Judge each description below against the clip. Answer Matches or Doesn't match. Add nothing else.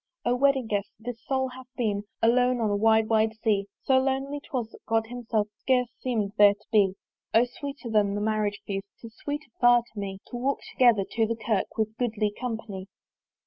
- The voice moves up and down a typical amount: Matches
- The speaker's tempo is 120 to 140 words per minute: Doesn't match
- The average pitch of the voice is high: Matches